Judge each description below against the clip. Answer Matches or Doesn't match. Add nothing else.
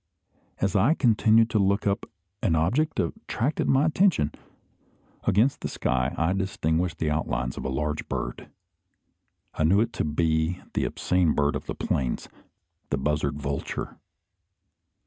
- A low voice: Matches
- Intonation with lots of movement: Matches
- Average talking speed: Matches